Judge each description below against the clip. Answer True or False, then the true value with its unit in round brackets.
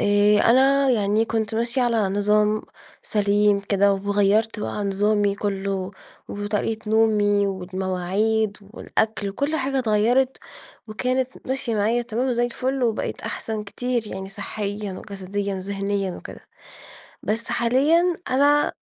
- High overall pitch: True (210 Hz)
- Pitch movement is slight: False (3.0 semitones)